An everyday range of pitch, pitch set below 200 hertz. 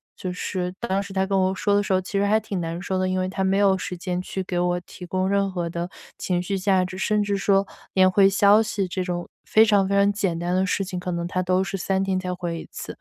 No: narrow, 1.6 semitones; high, 190 Hz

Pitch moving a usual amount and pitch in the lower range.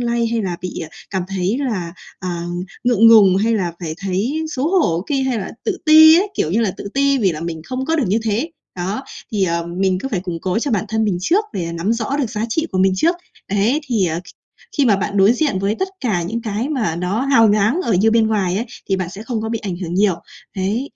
No: average, 4.8 semitones; high, 210 Hz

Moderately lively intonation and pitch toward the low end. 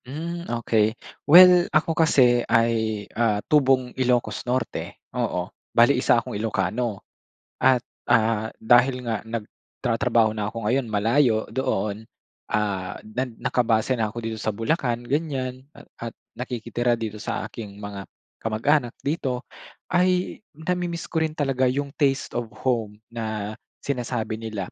Yes: average, 3.5 semitones; low, 120 Hz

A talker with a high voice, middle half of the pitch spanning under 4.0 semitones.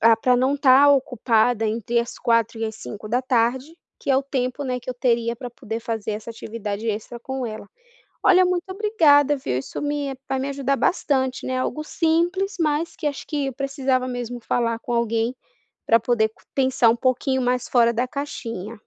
Yes: very high, 250 Hz; average, 3.3 semitones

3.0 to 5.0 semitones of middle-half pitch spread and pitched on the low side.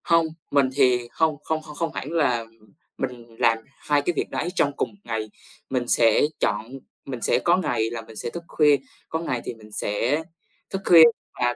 No: wide, 5.4 semitones; low, 130 Hz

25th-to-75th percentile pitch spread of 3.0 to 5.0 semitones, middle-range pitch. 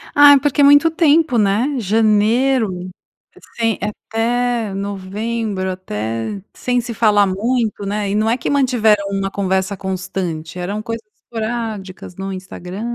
No: average, 3.7 semitones; high, 210 Hz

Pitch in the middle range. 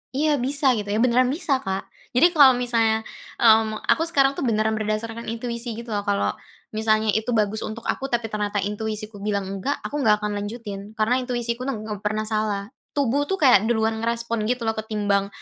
No: high, 220 Hz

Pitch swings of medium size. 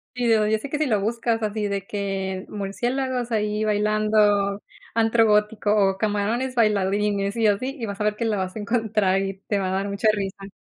No: narrow, 2.0 semitones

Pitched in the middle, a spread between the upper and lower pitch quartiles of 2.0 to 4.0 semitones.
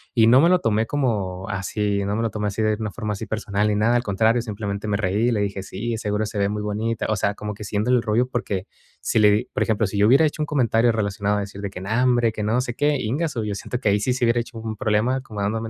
No: low, 110 Hz; narrow, 2.4 semitones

